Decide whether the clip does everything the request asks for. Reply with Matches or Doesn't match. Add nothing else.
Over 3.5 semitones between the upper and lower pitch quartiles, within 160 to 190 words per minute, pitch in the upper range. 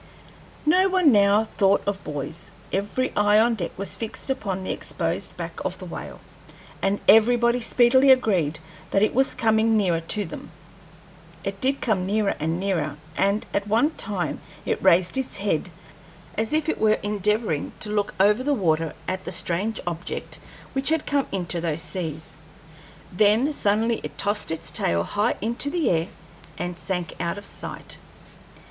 Matches